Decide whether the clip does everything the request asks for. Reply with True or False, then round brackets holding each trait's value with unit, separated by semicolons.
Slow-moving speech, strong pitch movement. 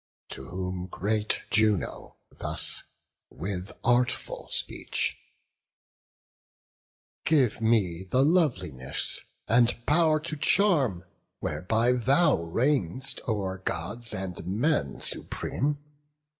True (90 wpm; 6.9 semitones)